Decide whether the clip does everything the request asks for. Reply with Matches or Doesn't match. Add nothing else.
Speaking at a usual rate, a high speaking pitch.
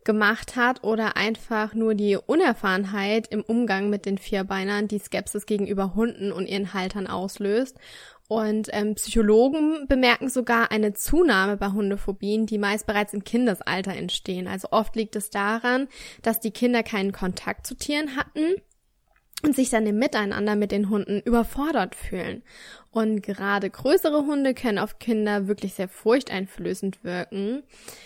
Matches